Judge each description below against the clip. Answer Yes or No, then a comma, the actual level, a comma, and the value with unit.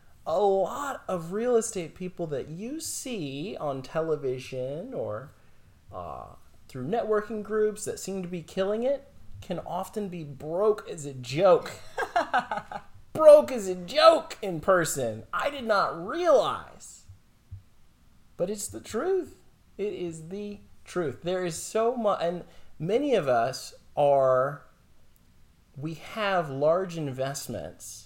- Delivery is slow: Yes, slow, 130 wpm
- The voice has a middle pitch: Yes, medium, 180 Hz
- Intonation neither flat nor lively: No, wide, 7.2 semitones